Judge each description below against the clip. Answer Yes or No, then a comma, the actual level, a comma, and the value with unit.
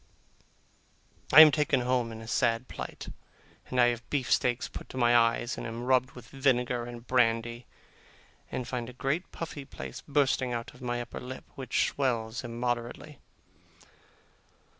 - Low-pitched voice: Yes, low, 125 Hz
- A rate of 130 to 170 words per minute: Yes, average, 160 wpm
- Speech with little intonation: Yes, narrow, 1.6 semitones